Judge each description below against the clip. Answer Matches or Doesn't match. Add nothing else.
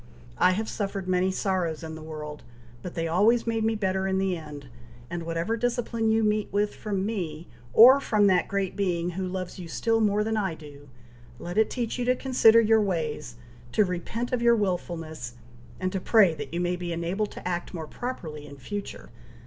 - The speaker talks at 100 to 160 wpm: Doesn't match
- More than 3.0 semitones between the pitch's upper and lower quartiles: Matches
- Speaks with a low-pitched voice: Doesn't match